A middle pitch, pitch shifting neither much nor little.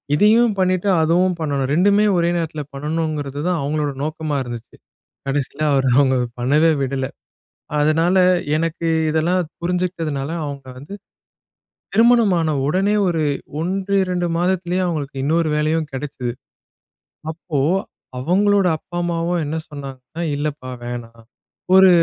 Yes: medium, 160 Hz; average, 4.1 semitones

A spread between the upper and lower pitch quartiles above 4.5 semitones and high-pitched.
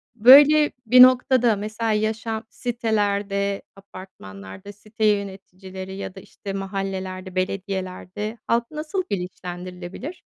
No: average, 3.3 semitones; high, 200 Hz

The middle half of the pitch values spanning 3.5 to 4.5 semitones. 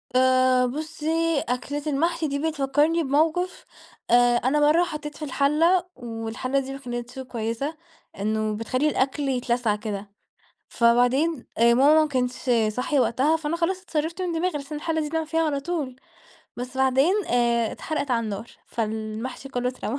Yes: average, 4.2 semitones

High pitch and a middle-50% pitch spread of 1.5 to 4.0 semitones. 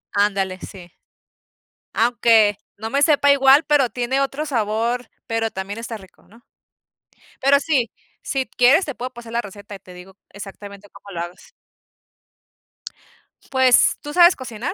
No: high, 230 Hz; average, 4.8 semitones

